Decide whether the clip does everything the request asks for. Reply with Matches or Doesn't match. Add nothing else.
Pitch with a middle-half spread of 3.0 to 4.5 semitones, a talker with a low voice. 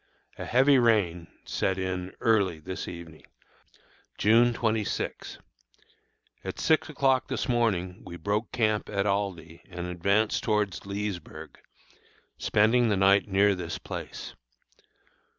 Matches